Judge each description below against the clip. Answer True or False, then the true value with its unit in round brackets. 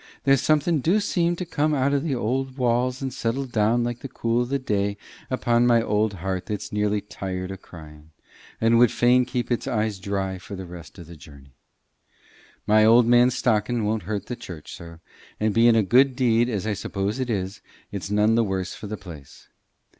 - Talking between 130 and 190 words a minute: False (205 wpm)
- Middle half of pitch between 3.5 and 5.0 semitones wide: True (4.1 semitones)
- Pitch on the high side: False (110 Hz)